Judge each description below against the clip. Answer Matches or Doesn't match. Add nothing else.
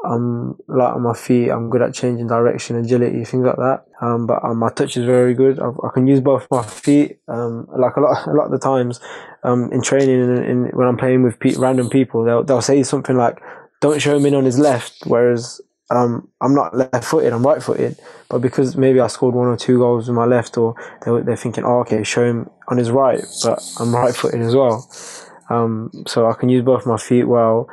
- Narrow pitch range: Matches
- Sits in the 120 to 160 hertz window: Matches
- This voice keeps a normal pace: Doesn't match